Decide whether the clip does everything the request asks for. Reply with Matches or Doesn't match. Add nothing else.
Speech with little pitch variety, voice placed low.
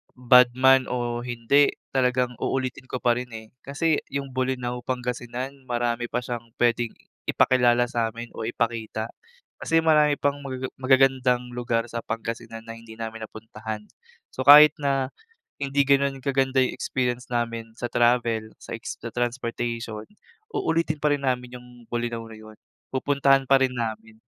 Matches